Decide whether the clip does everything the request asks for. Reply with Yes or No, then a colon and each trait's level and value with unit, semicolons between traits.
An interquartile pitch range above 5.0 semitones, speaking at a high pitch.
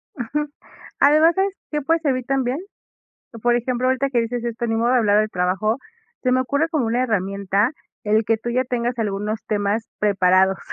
No: average, 3.6 semitones; high, 235 Hz